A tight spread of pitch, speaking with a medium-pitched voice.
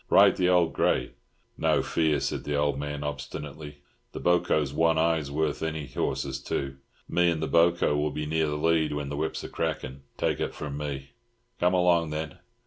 No: narrow, 2.3 semitones; very low, 75 Hz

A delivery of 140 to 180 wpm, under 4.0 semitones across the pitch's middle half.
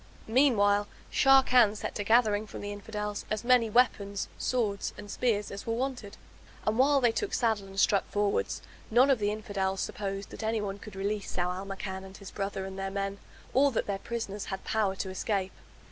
No: average, 190 wpm; narrow, 2.5 semitones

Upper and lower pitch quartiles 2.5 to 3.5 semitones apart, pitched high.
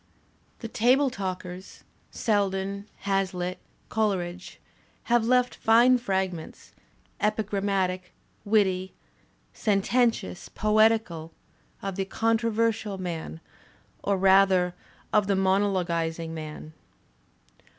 Yes: average, 3.1 semitones; high, 195 Hz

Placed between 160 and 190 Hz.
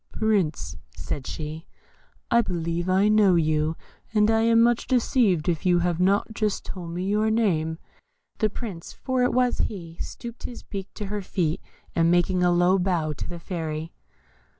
Yes: medium, 185 Hz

